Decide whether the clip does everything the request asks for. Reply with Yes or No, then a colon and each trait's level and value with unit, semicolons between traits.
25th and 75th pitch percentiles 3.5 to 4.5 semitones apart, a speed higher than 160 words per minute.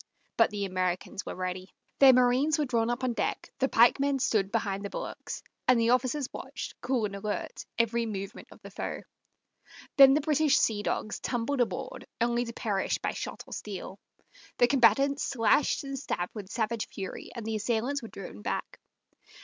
Yes: average, 4.2 semitones; average, 180 wpm